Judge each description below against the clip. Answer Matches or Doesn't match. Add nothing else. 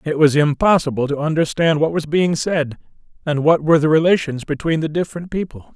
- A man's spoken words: Matches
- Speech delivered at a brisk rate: Doesn't match